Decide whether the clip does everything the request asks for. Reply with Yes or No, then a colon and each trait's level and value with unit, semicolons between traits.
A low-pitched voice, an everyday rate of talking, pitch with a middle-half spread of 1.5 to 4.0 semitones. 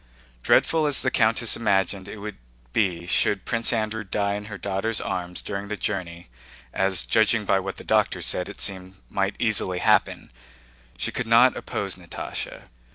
Yes: low, 100 Hz; average, 160 wpm; average, 3.2 semitones